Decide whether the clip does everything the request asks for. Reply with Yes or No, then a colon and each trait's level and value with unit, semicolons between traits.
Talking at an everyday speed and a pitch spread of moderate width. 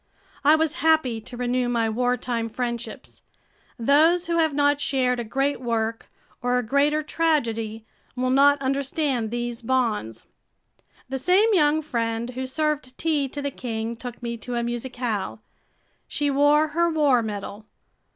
Yes: average, 150 wpm; average, 3.8 semitones